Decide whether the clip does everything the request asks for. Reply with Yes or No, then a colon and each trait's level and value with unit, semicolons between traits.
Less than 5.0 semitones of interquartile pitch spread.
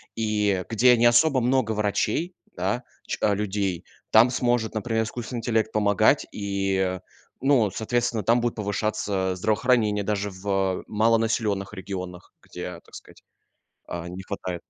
Yes: average, 3.1 semitones